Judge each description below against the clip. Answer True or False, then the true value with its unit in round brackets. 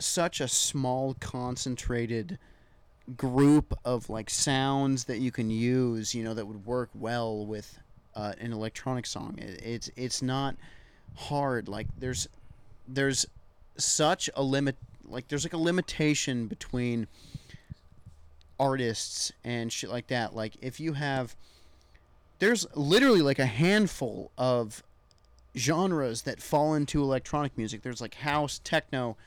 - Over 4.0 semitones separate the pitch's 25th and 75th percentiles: False (3.7 semitones)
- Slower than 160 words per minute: True (135 wpm)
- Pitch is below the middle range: True (125 Hz)